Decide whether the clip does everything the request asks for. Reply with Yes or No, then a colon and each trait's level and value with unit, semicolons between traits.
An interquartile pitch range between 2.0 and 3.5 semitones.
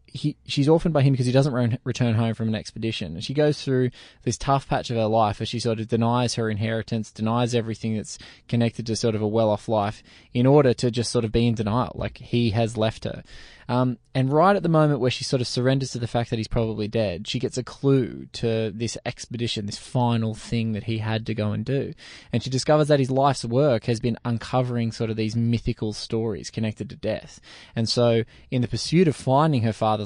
Yes: narrow, 2.5 semitones